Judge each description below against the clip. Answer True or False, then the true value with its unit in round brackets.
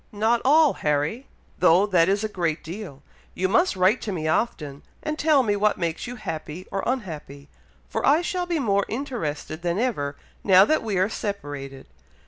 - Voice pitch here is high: True (195 Hz)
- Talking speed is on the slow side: False (180 wpm)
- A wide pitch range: True (7.1 semitones)